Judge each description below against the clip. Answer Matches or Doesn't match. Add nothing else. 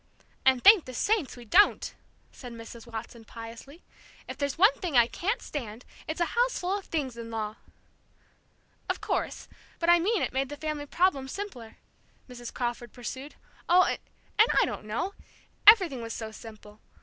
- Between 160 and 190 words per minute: Matches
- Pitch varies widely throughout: Matches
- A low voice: Doesn't match